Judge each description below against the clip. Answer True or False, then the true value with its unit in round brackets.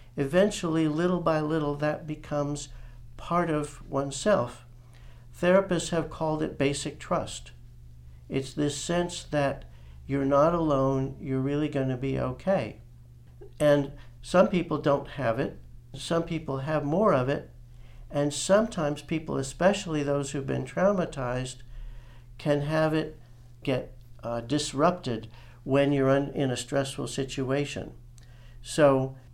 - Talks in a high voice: False (140 Hz)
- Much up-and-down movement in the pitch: False (4.2 semitones)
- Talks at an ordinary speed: False (125 wpm)